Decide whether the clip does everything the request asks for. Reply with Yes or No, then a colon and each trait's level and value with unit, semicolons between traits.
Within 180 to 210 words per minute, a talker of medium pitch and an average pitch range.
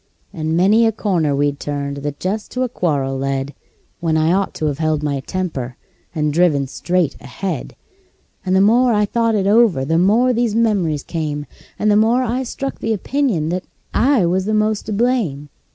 No: average, 190 wpm; medium, 180 Hz; wide, 6.8 semitones